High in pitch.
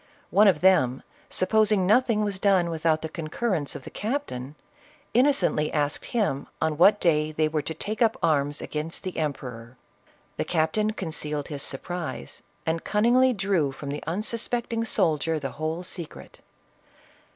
No: medium, 165 Hz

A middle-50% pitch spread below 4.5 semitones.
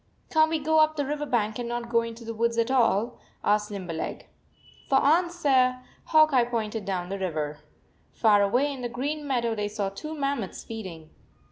No: wide, 5.4 semitones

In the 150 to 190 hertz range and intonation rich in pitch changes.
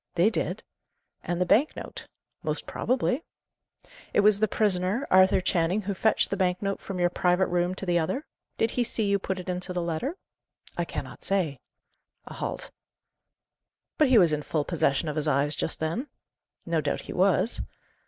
No: medium, 185 Hz; average, 3.4 semitones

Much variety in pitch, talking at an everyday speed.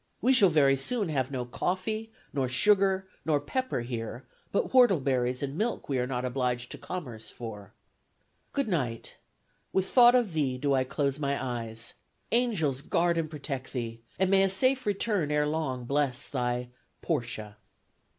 Yes: wide, 7.3 semitones; average, 160 wpm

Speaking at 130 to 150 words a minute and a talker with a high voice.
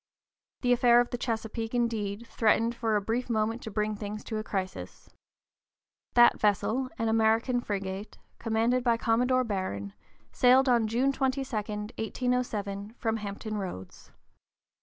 Yes: average, 140 wpm; high, 225 Hz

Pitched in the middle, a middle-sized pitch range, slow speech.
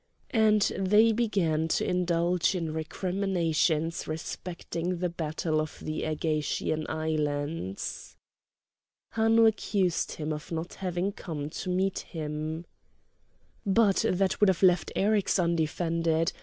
Yes: medium, 170 Hz; average, 3.4 semitones; slow, 115 wpm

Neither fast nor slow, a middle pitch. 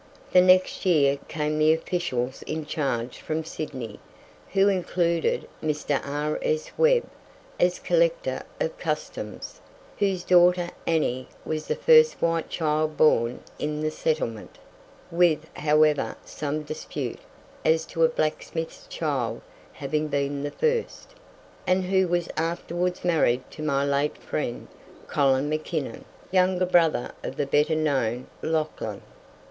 No: slow, 125 wpm; medium, 155 Hz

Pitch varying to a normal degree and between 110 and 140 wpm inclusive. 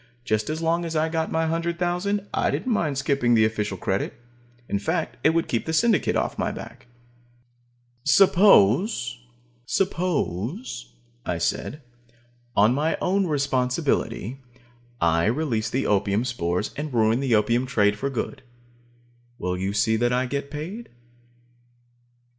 No: wide, 6.8 semitones; slow, 135 wpm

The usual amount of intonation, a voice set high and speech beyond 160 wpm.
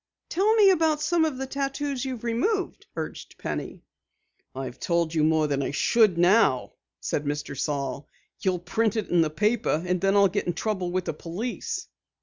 No: wide, 8.4 semitones; high, 195 Hz; average, 180 wpm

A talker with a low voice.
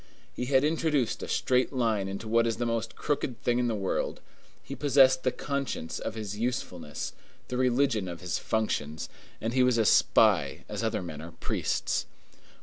Yes: low, 115 Hz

